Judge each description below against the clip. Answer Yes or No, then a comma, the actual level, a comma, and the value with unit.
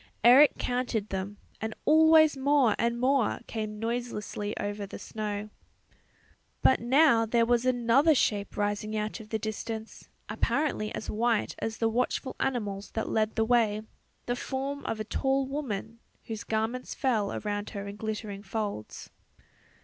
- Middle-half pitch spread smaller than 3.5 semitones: Yes, average, 3.0 semitones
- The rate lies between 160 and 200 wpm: No, average, 150 wpm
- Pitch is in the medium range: No, high, 225 Hz